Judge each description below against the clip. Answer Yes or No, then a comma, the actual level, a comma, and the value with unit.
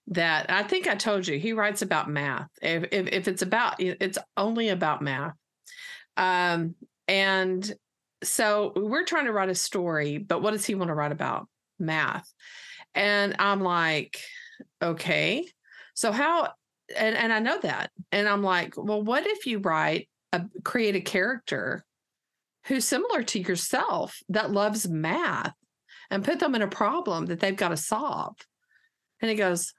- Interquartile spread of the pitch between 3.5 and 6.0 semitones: Yes, average, 3.9 semitones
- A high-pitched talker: Yes, high, 200 Hz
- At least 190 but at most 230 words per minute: No, average, 165 wpm